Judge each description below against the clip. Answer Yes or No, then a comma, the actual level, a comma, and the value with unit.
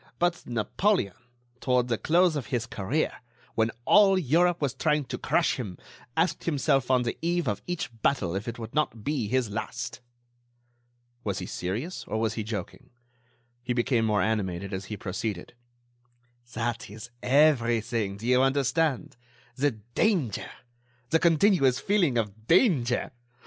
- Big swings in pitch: Yes, wide, 5.8 semitones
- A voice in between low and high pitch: No, low, 125 Hz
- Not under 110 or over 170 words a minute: Yes, average, 150 wpm